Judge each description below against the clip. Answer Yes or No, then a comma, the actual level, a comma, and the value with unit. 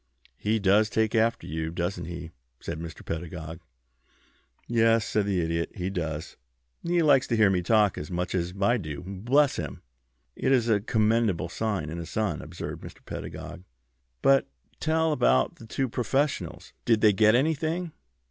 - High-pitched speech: No, low, 105 Hz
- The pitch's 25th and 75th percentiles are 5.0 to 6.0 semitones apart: Yes, wide, 5.5 semitones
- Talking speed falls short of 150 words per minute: No, average, 165 wpm